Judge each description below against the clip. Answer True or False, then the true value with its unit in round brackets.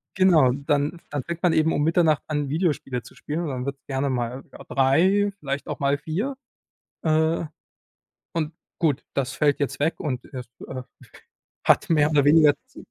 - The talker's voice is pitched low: False (145 Hz)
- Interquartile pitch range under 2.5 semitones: False (2.9 semitones)